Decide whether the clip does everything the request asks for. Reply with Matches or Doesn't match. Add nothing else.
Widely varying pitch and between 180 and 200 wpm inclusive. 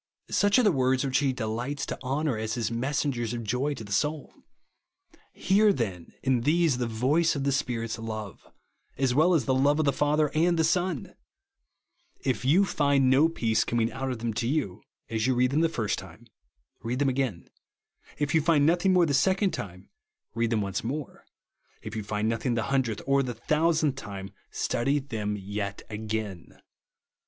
Doesn't match